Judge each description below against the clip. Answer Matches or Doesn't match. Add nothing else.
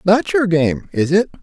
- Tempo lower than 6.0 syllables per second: Matches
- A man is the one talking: Matches